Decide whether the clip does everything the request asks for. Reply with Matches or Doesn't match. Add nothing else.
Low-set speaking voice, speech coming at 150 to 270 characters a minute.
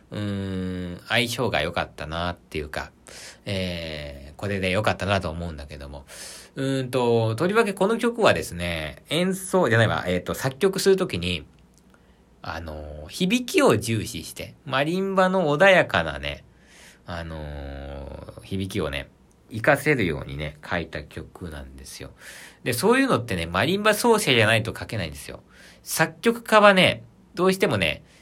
Doesn't match